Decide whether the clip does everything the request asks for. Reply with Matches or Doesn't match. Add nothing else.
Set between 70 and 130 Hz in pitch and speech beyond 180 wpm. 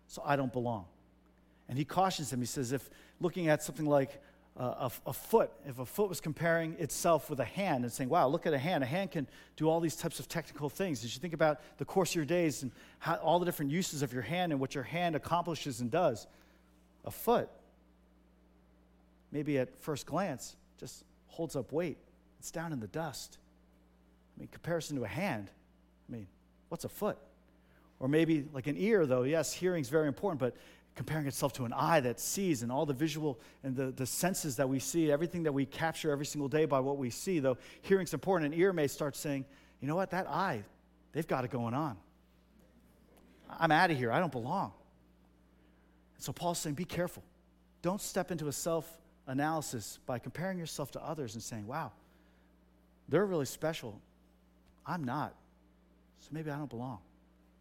Doesn't match